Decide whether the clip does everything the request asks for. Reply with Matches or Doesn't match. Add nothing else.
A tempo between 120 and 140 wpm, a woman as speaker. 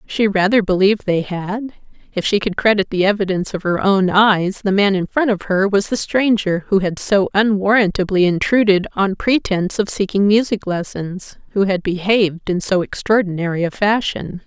Doesn't match